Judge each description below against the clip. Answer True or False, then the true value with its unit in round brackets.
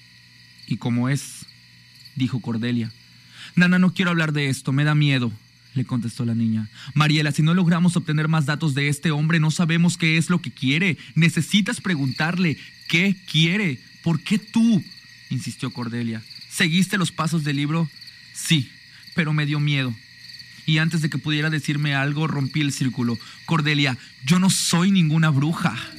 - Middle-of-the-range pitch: True (150 Hz)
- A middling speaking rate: True (160 wpm)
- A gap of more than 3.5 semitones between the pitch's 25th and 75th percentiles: True (4.7 semitones)